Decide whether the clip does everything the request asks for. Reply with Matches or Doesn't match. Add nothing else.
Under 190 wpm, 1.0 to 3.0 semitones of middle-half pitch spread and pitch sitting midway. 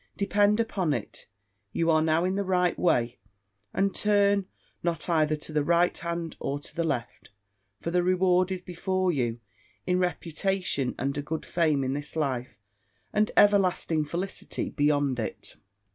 Doesn't match